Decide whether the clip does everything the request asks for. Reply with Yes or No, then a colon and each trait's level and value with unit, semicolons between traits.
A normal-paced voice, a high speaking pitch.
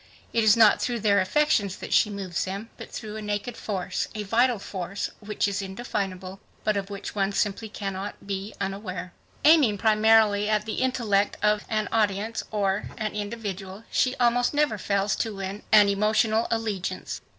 Yes: average, 170 wpm; high, 210 Hz